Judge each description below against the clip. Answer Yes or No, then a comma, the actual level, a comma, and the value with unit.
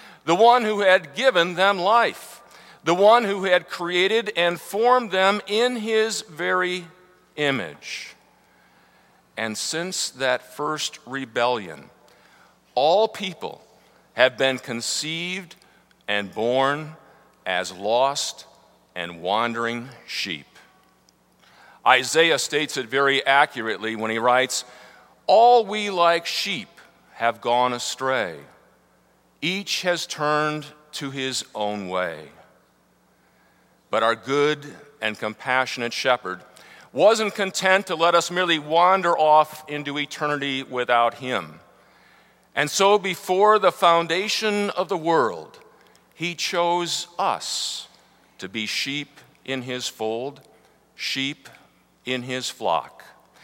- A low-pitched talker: No, medium, 150 Hz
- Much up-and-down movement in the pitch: Yes, wide, 6.7 semitones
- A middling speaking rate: No, slow, 110 wpm